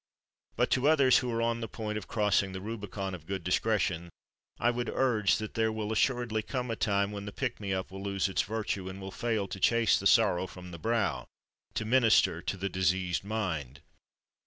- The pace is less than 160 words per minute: No, fast, 205 wpm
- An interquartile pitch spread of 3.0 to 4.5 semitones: Yes, average, 3.3 semitones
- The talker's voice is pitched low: Yes, low, 105 Hz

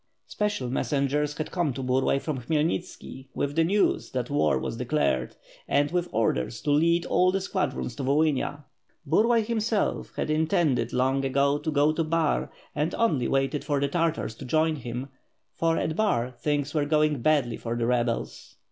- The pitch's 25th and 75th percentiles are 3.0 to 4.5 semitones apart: Yes, average, 3.8 semitones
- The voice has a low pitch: No, medium, 145 Hz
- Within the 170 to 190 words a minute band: Yes, average, 175 wpm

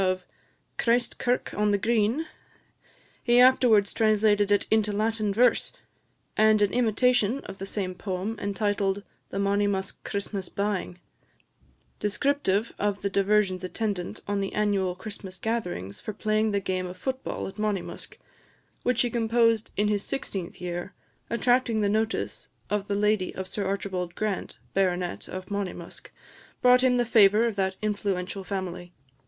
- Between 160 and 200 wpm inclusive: No, average, 150 wpm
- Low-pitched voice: No, high, 205 Hz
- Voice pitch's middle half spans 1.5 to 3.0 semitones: Yes, narrow, 2.5 semitones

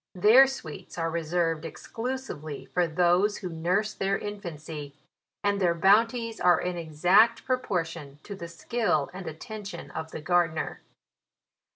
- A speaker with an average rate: Yes, average, 150 wpm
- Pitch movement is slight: No, average, 4.3 semitones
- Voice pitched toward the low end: No, medium, 175 Hz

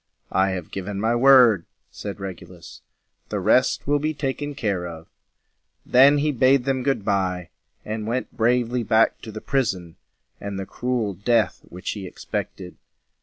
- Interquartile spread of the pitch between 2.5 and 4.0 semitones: No, average, 5.2 semitones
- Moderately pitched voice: No, low, 110 Hz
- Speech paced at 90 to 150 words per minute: No, average, 165 wpm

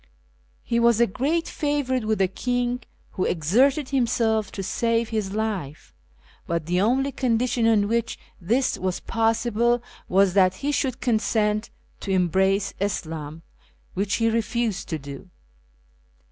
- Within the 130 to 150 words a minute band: Yes, slow, 135 wpm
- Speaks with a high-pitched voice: Yes, high, 220 Hz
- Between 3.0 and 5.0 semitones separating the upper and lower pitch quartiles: Yes, average, 4.0 semitones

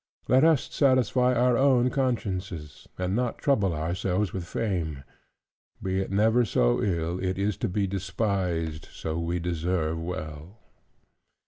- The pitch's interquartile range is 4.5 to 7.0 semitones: Yes, wide, 5.4 semitones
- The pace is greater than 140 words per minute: No, slow, 135 wpm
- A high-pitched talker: No, very low, 95 Hz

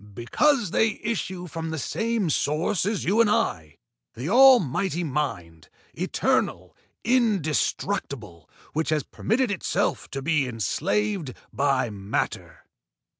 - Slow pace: Yes, slow, 115 wpm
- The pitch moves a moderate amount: No, wide, 8.1 semitones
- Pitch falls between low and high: Yes, medium, 165 Hz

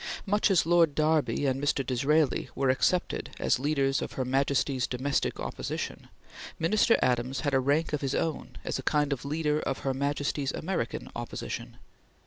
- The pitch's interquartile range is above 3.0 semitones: No, narrow, 2.6 semitones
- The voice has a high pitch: No, medium, 140 Hz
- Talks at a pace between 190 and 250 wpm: No, average, 165 wpm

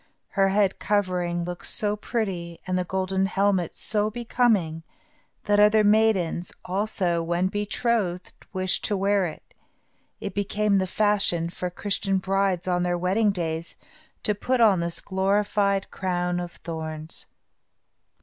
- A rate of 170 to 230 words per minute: No, average, 140 wpm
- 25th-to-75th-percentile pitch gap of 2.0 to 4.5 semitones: Yes, average, 2.7 semitones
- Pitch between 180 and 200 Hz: Yes, high, 190 Hz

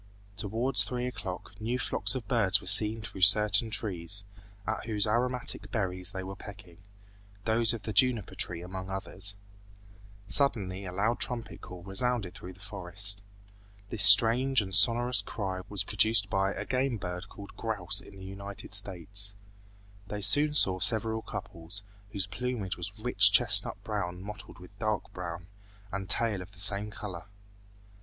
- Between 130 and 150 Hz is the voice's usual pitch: No, low, 100 Hz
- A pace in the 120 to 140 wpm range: No, average, 155 wpm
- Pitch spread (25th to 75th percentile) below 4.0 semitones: Yes, average, 3.0 semitones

